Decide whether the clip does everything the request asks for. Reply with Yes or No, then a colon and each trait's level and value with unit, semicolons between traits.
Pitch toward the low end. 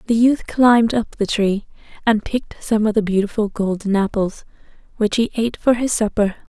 No: high, 220 Hz